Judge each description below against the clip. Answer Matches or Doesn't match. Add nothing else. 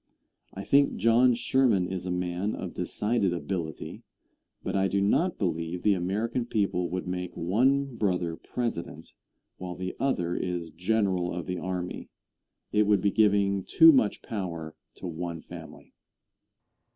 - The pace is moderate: Matches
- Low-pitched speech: Matches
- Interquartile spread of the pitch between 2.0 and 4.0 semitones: Matches